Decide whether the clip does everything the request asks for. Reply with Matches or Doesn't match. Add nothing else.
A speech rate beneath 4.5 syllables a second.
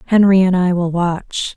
Matches